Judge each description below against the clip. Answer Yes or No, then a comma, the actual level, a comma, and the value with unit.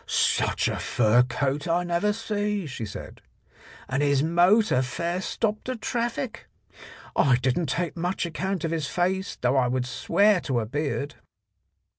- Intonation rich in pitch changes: Yes, wide, 6.6 semitones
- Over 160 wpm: No, average, 155 wpm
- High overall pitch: No, medium, 170 Hz